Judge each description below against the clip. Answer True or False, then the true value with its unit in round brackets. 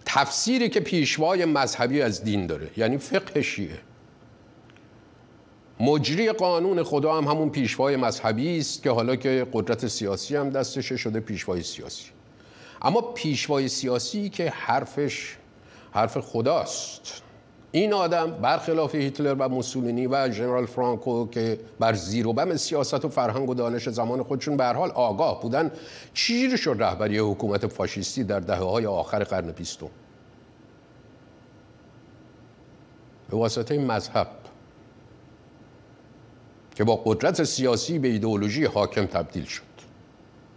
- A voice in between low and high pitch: False (125 Hz)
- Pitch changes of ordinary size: True (4.5 semitones)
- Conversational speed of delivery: True (125 wpm)